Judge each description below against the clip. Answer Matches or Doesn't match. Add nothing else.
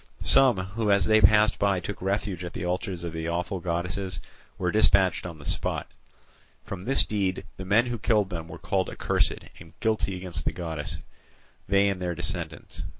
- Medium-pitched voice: Doesn't match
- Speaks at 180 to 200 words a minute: Matches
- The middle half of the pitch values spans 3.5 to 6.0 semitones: Doesn't match